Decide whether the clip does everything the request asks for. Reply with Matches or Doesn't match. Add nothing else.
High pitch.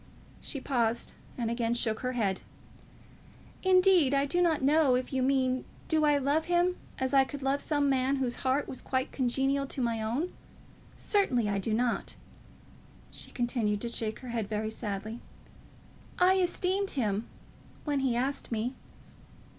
Matches